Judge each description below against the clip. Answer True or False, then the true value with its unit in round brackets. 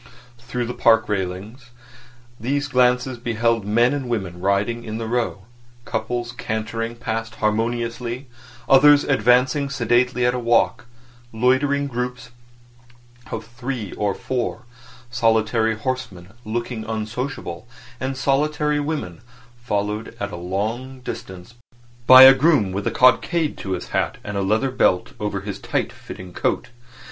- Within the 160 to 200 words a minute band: False (135 wpm)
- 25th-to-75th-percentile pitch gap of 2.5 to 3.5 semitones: True (3.1 semitones)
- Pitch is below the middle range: True (120 Hz)